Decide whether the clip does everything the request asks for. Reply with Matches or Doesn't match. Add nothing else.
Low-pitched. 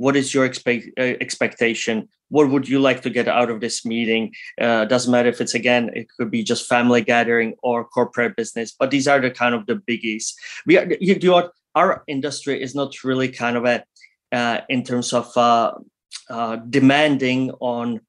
Matches